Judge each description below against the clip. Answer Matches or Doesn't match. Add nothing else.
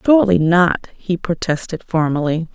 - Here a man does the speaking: Doesn't match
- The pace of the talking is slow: Matches